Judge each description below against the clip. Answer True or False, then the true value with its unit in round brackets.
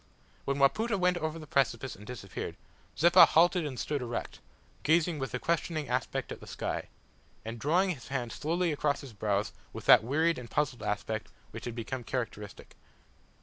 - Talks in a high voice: False (140 Hz)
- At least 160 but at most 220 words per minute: True (175 wpm)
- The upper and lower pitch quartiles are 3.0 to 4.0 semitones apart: False (5.6 semitones)